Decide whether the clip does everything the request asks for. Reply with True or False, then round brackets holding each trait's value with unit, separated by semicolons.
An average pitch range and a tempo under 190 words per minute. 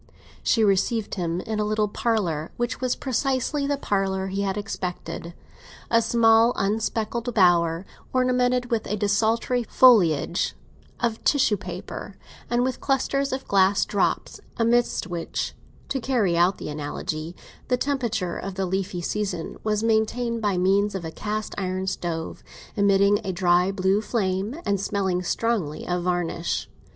True (4.1 semitones; 140 wpm)